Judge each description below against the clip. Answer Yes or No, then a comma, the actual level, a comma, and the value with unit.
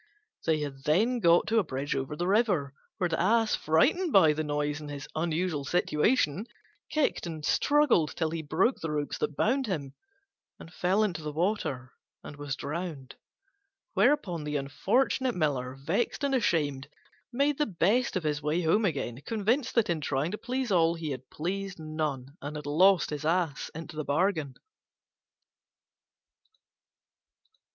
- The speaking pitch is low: No, medium, 165 Hz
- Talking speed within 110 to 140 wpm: No, average, 160 wpm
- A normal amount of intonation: No, wide, 5.7 semitones